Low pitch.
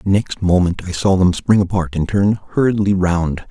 Yes: very low, 95 Hz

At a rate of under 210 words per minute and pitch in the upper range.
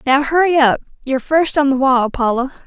Yes: average, 200 wpm; very high, 275 Hz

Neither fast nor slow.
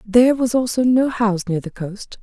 No: fast, 215 wpm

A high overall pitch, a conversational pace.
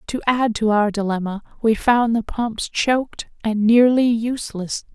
Yes: high, 225 Hz; average, 160 wpm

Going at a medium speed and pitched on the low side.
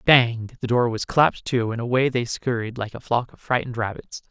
No: fast, 225 wpm; low, 120 Hz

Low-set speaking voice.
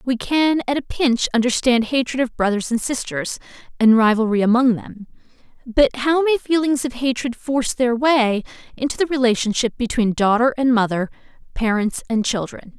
No: high, 245 Hz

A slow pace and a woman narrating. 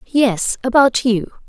Yes: slow, 120 wpm; female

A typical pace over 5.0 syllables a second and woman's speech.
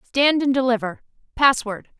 No: 4.7 syllables/s; female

